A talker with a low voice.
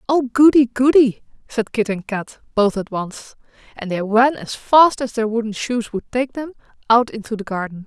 No: high, 235 Hz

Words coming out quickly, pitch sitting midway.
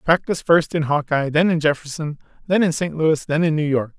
Yes: fast, 225 wpm; medium, 155 Hz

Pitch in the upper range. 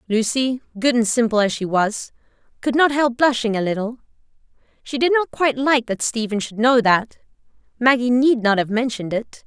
Yes: high, 240 Hz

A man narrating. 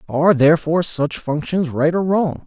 Yes: male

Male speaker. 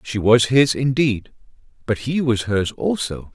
Yes: male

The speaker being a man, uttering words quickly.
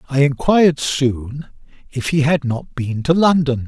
No: male; average, 165 wpm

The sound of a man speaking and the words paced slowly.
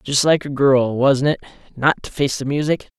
No: male; average, 200 wpm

